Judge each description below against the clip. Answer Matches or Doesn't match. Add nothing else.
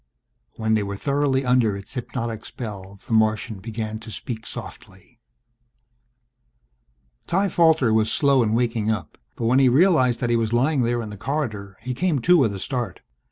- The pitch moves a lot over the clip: Doesn't match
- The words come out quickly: Doesn't match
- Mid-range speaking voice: Doesn't match